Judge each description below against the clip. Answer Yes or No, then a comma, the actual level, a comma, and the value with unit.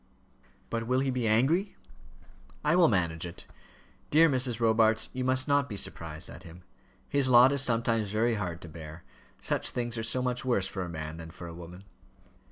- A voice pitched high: No, low, 115 Hz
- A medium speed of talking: Yes, average, 190 wpm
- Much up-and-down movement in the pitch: Yes, wide, 6.6 semitones